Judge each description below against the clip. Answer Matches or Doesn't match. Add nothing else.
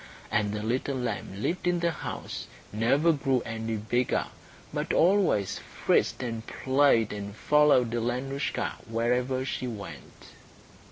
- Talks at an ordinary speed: Doesn't match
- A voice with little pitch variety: Doesn't match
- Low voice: Matches